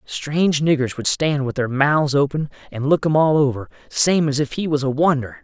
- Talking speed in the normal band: No, fast, 220 wpm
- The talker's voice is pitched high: No, medium, 140 Hz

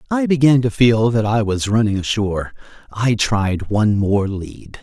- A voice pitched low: Yes, low, 110 Hz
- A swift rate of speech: No, average, 175 wpm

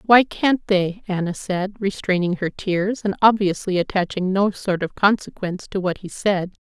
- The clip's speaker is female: Yes, female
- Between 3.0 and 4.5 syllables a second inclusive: No, 4.7 syllables/s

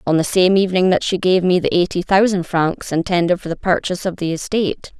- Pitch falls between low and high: Yes, medium, 180 Hz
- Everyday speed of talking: No, fast, 230 wpm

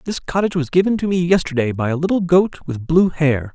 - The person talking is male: Yes, male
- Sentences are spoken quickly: Yes, fast, 235 wpm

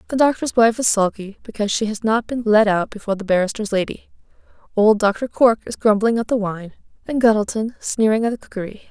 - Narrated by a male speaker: No, female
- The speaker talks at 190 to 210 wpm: Yes, average, 200 wpm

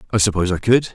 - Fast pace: Yes, fast, 255 wpm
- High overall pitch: No, low, 100 Hz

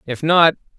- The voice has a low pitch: No, medium, 155 Hz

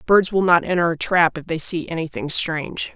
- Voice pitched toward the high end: No, medium, 170 Hz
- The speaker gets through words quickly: Yes, fast, 225 wpm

